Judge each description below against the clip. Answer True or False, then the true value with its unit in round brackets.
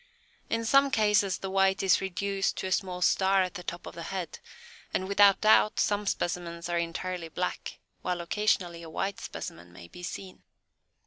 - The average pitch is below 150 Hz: False (185 Hz)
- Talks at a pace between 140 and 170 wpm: False (180 wpm)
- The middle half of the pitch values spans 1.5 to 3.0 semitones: True (2.5 semitones)